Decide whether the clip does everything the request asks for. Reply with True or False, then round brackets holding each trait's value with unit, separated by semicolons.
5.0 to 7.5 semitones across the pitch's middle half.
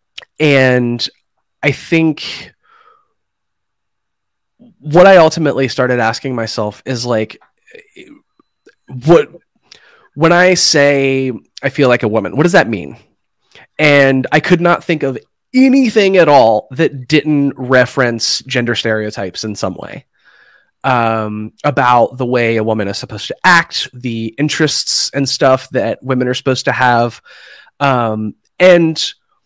True (5.5 semitones)